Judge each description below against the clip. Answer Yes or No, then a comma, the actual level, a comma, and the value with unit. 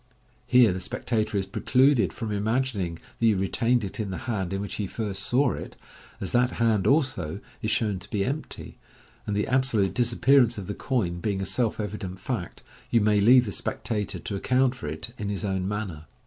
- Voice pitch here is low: Yes, low, 105 Hz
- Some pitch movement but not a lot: Yes, average, 4.0 semitones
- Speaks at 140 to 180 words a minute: No, average, 200 wpm